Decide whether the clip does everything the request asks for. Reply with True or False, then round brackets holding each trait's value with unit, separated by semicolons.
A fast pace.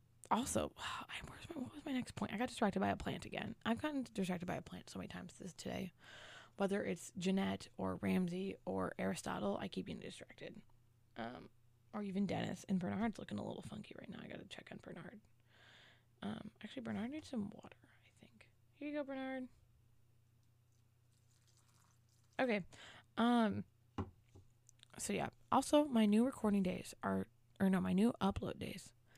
False (170 wpm)